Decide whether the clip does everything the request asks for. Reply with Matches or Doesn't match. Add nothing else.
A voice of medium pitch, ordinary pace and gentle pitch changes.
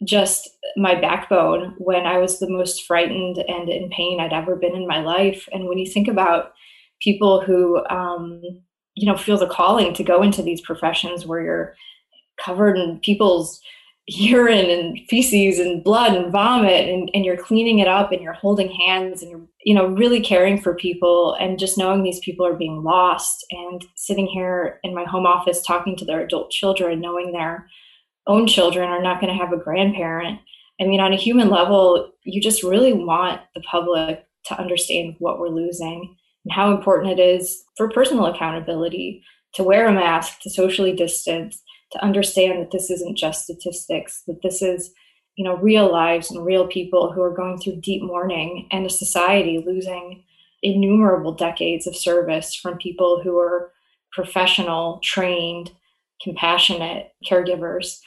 Matches